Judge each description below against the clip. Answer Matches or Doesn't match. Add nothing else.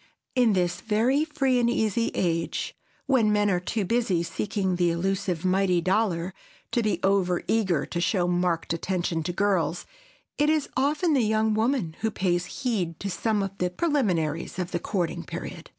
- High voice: Matches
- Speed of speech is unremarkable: Matches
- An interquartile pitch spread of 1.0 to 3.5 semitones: Doesn't match